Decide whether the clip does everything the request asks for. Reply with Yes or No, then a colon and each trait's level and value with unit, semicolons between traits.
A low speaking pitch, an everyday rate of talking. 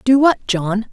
No: high, 230 Hz; average, 195 wpm